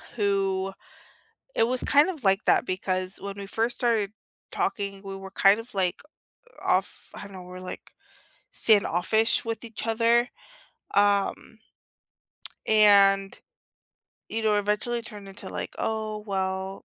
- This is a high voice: Yes, high, 200 Hz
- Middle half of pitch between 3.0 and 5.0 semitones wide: No, narrow, 2.4 semitones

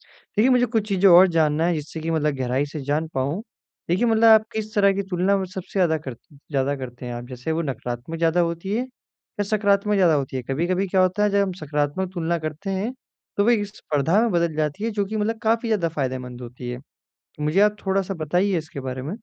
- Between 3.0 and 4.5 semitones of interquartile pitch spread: No, wide, 5.5 semitones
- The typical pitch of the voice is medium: Yes, medium, 170 Hz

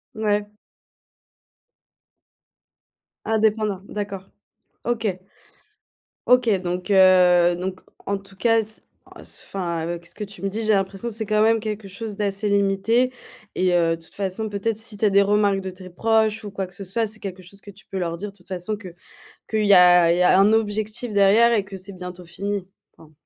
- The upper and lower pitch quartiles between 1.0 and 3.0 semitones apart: Yes, average, 2.7 semitones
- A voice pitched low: No, high, 200 Hz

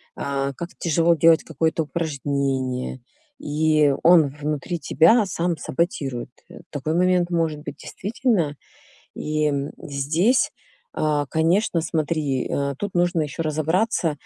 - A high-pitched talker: No, medium, 155 Hz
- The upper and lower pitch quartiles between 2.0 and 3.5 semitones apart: Yes, average, 3.0 semitones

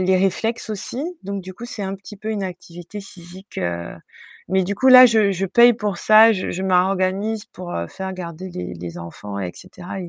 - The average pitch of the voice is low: No, high, 190 Hz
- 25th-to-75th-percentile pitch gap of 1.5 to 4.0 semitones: Yes, average, 2.9 semitones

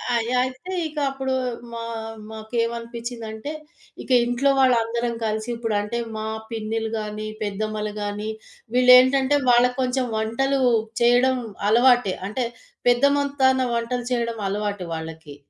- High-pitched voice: Yes, high, 235 Hz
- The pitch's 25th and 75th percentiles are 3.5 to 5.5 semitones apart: No, average, 2.9 semitones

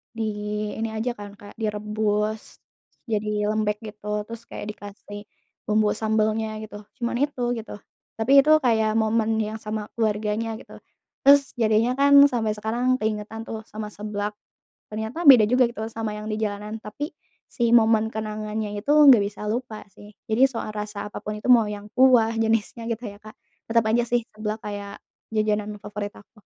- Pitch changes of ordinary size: No, narrow, 1.4 semitones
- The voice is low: No, high, 215 Hz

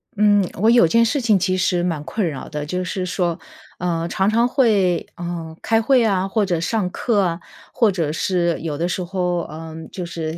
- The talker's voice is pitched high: No, medium, 180 Hz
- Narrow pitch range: No, average, 3.7 semitones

